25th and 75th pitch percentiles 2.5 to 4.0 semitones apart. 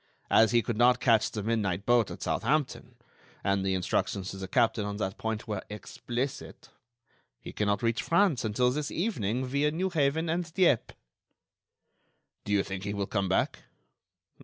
No: average, 5.3 semitones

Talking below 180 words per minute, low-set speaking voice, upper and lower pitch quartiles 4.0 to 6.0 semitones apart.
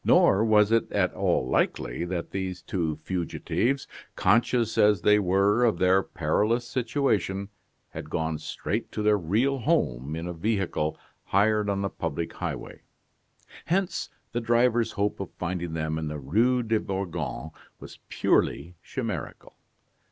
Yes: average, 145 wpm; low, 100 Hz; average, 5.0 semitones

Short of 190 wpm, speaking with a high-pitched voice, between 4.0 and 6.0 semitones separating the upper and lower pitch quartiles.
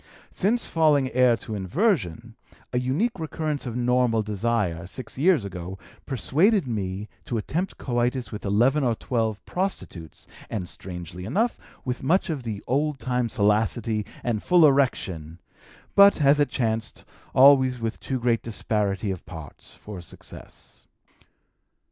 No: slow, 135 wpm; low, 120 Hz; average, 5.3 semitones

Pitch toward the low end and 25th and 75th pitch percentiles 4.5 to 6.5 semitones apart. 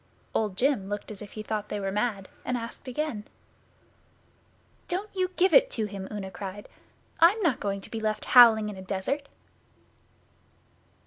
No: high, 215 Hz; average, 5.3 semitones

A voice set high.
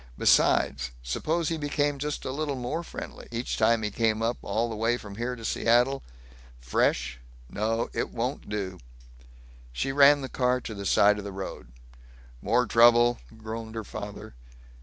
No: low, 115 Hz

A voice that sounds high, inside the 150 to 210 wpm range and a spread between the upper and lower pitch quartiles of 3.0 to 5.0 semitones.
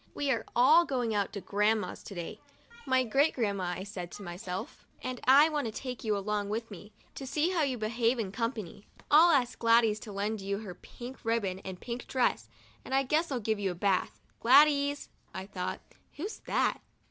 Yes: high, 225 Hz; fast, 205 wpm; average, 4.7 semitones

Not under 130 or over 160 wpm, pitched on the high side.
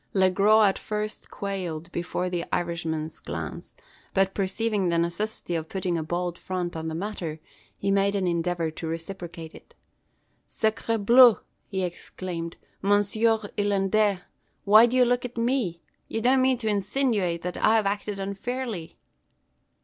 Yes: average, 150 wpm; high, 195 Hz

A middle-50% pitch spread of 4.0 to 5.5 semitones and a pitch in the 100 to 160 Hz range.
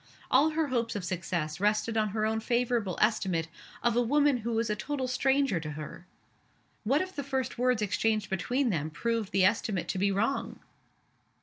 No: average, 4.7 semitones; high, 225 Hz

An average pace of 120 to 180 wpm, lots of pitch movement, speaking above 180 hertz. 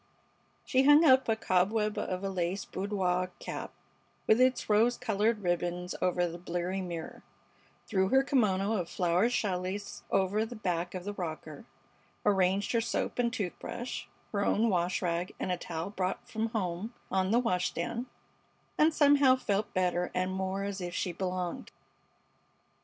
No: average, 160 wpm; average, 3.7 semitones; high, 190 Hz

